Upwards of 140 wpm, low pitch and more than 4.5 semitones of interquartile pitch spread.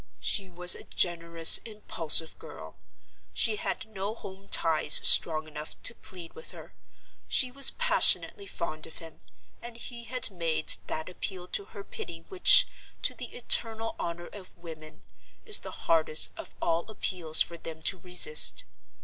No: average, 150 wpm; medium, 175 Hz; average, 5.0 semitones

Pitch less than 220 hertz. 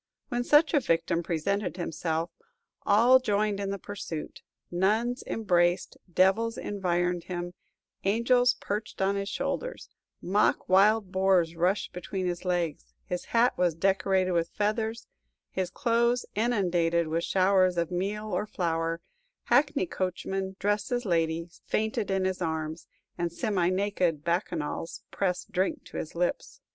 Yes: high, 190 Hz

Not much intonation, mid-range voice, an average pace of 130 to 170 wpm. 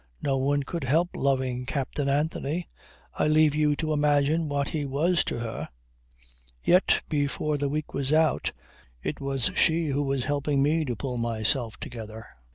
Yes: narrow, 2.3 semitones; medium, 145 Hz; average, 165 wpm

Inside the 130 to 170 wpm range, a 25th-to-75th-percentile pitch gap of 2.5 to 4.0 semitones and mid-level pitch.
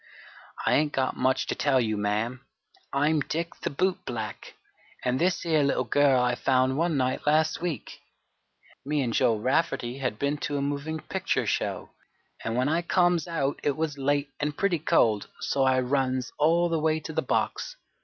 No: average, 185 wpm; average, 3.6 semitones; medium, 145 Hz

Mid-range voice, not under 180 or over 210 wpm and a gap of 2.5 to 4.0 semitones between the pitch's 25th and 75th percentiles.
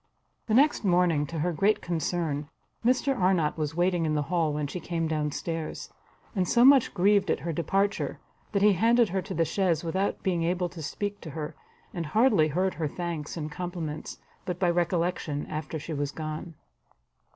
Yes: medium, 170 Hz; average, 185 wpm; average, 3.4 semitones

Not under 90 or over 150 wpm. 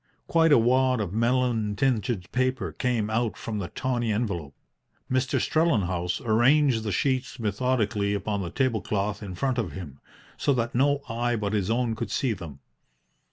No: average, 165 wpm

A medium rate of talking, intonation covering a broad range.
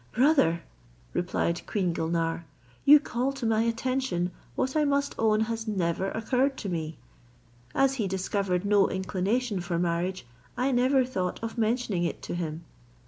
Yes: average, 150 wpm; wide, 6.2 semitones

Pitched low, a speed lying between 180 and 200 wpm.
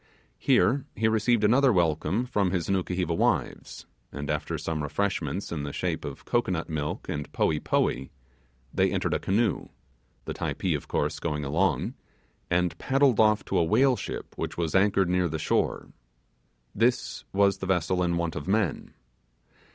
No: very low, 90 Hz; average, 160 wpm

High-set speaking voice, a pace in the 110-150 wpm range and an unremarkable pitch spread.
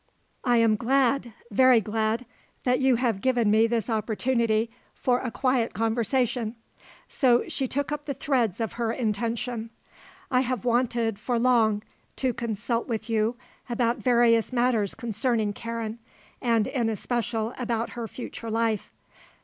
No: high, 235 Hz; average, 140 wpm; narrow, 2.0 semitones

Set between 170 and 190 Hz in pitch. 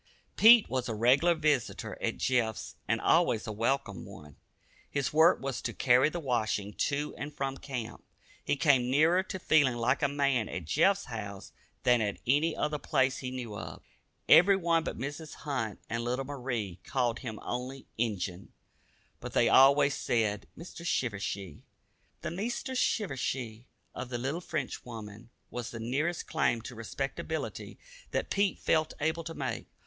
No: low, 130 Hz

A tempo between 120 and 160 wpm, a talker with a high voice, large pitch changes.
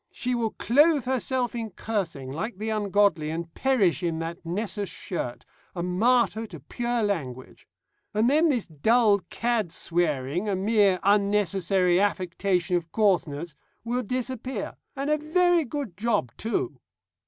Yes: average, 140 wpm; high, 205 Hz; wide, 5.7 semitones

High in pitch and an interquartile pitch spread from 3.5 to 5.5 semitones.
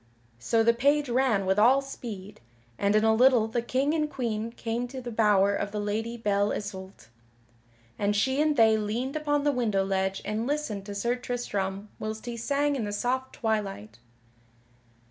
Yes: high, 225 Hz; average, 3.9 semitones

